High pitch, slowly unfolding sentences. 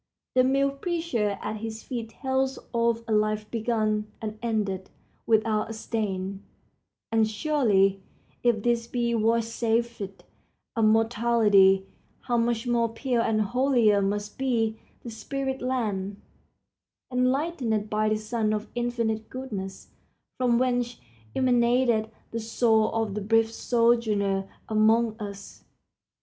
Yes: high, 225 Hz; slow, 120 wpm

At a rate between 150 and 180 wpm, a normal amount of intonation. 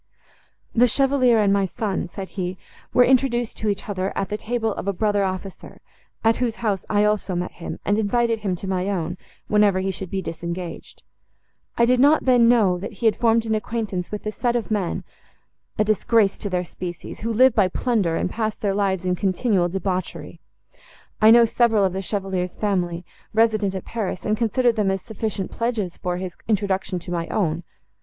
No: average, 195 wpm; average, 3.3 semitones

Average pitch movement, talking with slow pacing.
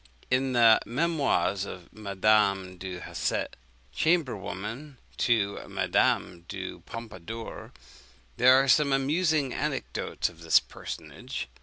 No: wide, 5.9 semitones; slow, 110 wpm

